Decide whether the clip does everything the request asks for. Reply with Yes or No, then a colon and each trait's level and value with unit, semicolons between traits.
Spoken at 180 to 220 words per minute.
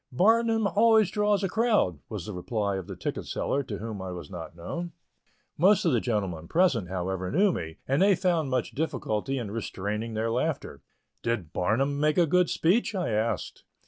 Yes: average, 185 wpm